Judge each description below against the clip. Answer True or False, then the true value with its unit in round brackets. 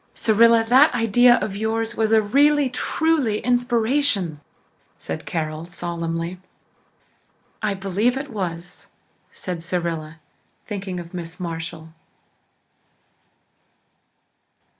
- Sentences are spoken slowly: True (95 wpm)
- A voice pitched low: False (200 Hz)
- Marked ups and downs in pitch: True (5.9 semitones)